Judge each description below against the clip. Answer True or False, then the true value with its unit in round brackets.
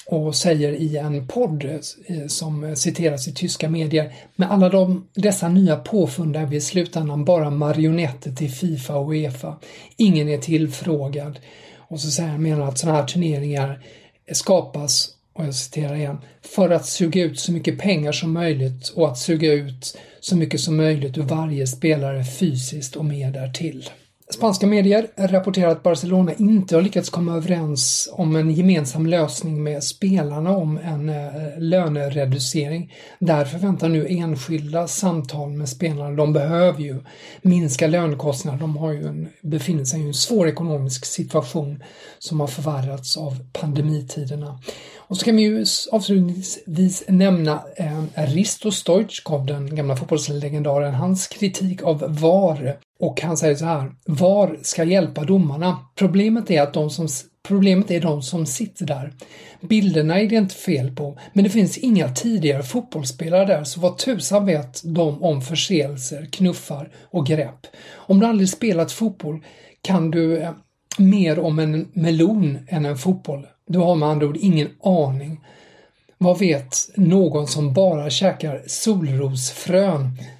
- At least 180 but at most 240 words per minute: False (150 wpm)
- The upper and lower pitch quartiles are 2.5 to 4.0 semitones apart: True (3.6 semitones)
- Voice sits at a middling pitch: True (160 Hz)